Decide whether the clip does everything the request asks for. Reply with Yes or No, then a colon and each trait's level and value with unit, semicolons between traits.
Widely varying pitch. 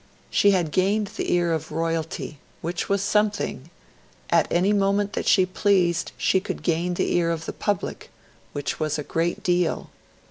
No: average, 3.3 semitones